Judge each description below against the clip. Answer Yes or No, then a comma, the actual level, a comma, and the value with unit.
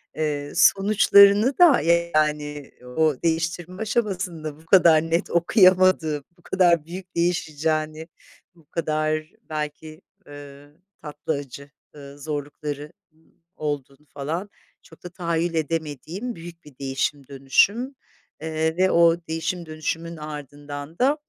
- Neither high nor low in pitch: Yes, medium, 160 Hz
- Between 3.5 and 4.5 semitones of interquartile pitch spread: No, average, 3.0 semitones